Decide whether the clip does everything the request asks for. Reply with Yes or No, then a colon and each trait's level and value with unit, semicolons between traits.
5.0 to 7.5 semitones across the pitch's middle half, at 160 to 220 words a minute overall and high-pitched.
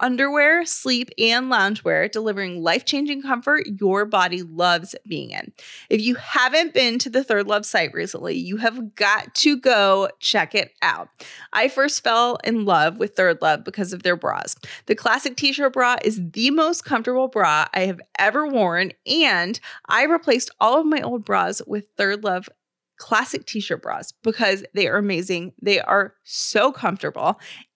Yes: wide, 5.5 semitones; average, 175 wpm; high, 225 Hz